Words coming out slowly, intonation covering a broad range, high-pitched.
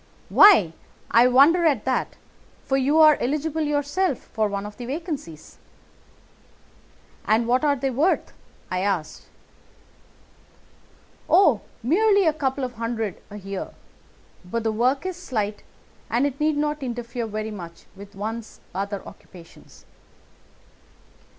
Yes: slow, 130 wpm; wide, 6.0 semitones; high, 245 Hz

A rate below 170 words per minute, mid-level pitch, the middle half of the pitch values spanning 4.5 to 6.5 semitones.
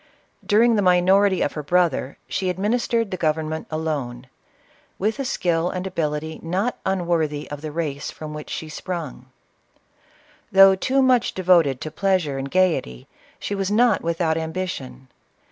No: average, 155 wpm; medium, 170 Hz; average, 4.0 semitones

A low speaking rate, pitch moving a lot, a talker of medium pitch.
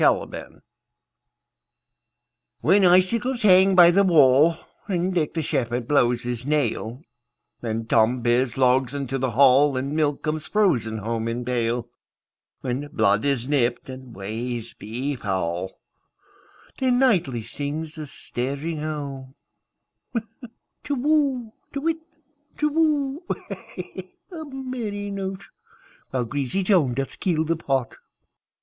Yes: slow, 105 wpm; wide, 7.8 semitones; medium, 145 Hz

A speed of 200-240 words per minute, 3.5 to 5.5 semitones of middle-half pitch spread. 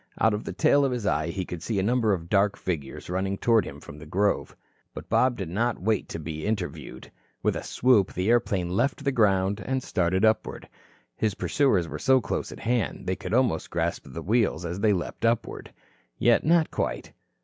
Yes: fast, 205 wpm; average, 4.6 semitones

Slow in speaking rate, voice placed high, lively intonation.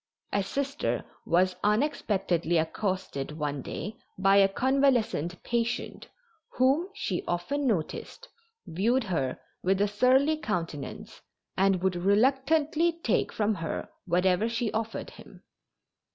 Yes: slow, 115 wpm; high, 205 Hz; wide, 6.5 semitones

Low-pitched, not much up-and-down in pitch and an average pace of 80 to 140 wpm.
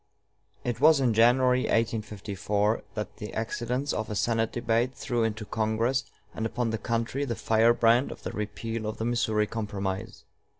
No: low, 115 Hz; narrow, 2.0 semitones; average, 160 wpm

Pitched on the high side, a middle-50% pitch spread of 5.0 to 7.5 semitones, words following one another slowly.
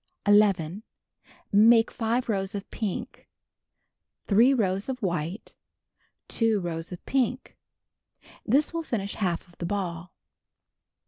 No: high, 205 Hz; average, 4.3 semitones; slow, 115 wpm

